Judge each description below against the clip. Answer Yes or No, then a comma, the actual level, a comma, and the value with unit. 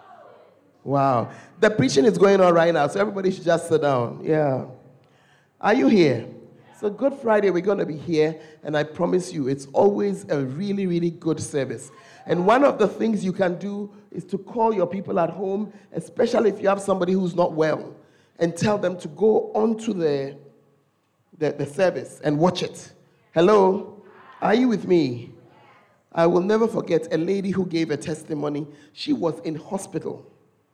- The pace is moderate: Yes, average, 180 wpm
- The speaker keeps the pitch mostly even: No, average, 4.1 semitones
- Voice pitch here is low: No, medium, 175 Hz